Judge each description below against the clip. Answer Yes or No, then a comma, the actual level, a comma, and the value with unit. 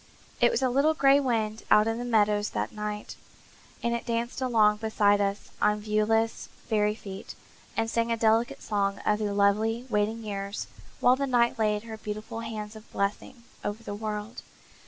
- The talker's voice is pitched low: No, high, 220 Hz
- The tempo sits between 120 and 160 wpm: No, average, 175 wpm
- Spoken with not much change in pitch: Yes, narrow, 1.8 semitones